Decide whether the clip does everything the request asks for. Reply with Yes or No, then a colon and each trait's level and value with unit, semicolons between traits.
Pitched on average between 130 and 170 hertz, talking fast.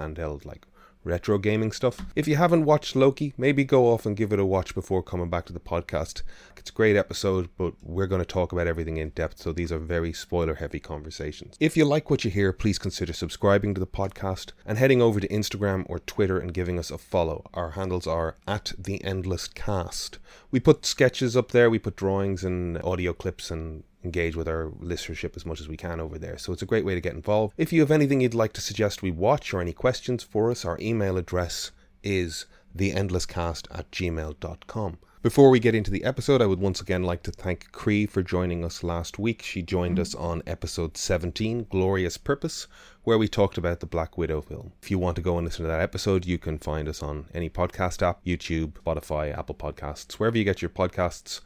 No: very low, 95 Hz; fast, 220 wpm